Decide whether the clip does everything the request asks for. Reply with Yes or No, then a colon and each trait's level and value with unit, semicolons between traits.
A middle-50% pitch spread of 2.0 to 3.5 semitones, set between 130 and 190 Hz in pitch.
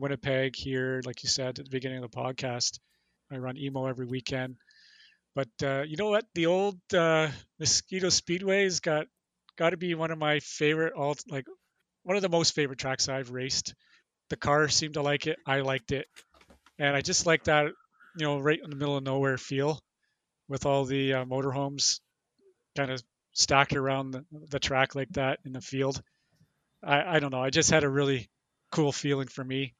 Yes: average, 2.8 semitones; medium, 140 Hz